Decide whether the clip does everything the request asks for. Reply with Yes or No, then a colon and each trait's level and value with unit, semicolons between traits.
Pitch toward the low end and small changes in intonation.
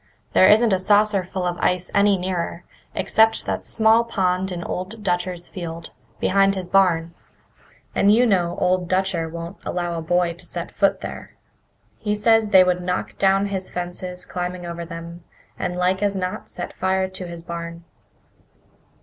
No: medium, 185 Hz; narrow, 2.0 semitones